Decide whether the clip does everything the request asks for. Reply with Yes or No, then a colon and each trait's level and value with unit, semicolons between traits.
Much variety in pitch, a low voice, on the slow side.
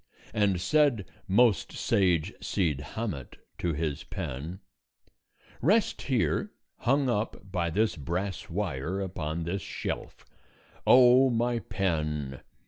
Yes: wide, 6.0 semitones; very low, 95 Hz; slow, 110 wpm